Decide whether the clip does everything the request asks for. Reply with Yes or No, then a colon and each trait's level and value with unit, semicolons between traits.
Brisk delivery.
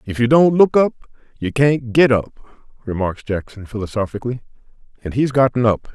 No: average, 160 wpm